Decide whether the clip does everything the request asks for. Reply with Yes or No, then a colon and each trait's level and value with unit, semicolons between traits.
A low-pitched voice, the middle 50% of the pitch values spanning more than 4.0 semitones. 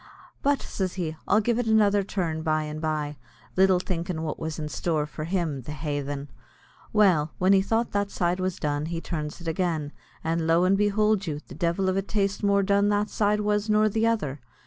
No: medium, 180 Hz; average, 4.5 semitones